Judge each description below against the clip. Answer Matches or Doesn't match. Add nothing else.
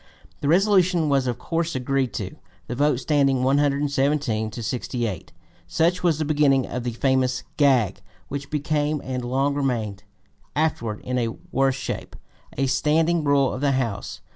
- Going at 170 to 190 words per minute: Doesn't match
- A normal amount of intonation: Matches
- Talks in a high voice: Doesn't match